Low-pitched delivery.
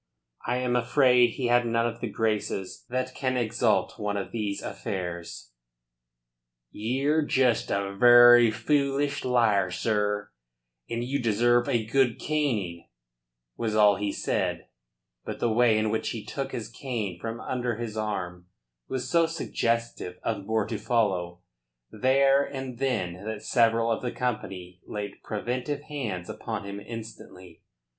Yes: low, 115 Hz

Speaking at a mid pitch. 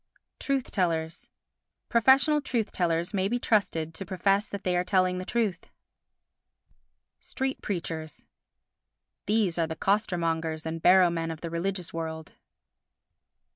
Yes: medium, 180 Hz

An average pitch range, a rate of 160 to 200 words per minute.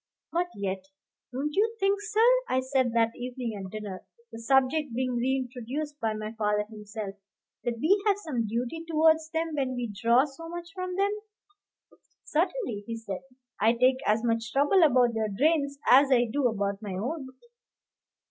No: wide, 5.7 semitones; average, 165 wpm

